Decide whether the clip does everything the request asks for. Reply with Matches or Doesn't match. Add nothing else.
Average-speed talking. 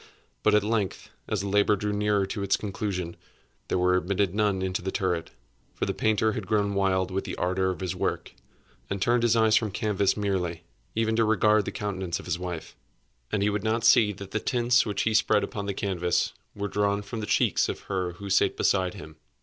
Doesn't match